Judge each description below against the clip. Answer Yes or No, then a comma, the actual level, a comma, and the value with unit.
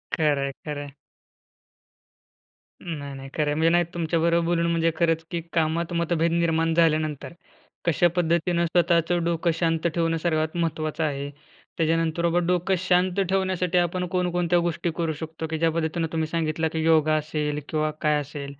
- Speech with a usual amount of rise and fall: No, narrow, 1.6 semitones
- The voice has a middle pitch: Yes, medium, 165 Hz